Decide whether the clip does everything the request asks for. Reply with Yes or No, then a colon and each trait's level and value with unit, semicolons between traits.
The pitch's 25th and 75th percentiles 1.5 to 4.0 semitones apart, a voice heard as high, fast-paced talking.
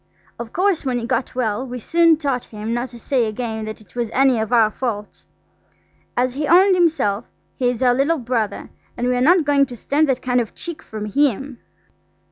Yes: average, 3.7 semitones; very high, 250 Hz; fast, 210 wpm